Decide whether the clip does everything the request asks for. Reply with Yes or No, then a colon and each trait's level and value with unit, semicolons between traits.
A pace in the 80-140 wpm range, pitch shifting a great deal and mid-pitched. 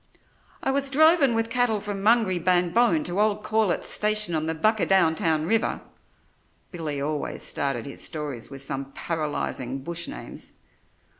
Yes: slow, 135 wpm; wide, 6.1 semitones; medium, 175 Hz